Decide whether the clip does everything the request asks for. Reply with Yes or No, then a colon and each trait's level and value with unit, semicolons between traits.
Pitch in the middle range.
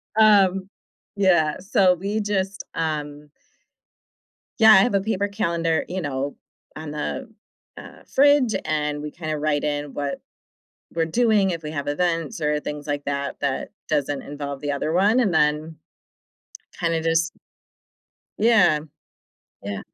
Yes: medium, 160 Hz